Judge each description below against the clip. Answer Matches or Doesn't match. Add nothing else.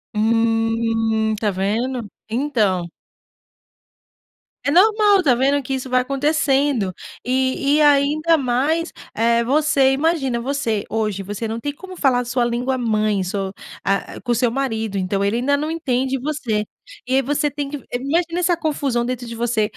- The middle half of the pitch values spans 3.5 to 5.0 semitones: Matches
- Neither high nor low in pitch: Doesn't match